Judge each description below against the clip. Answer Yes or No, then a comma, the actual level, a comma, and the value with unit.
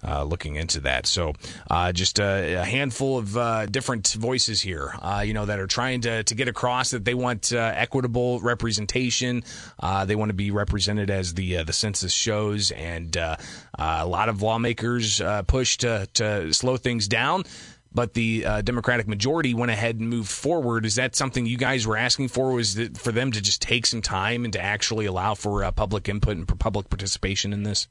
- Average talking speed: No, fast, 210 wpm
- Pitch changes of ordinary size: Yes, average, 3.3 semitones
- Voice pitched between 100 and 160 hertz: Yes, low, 110 Hz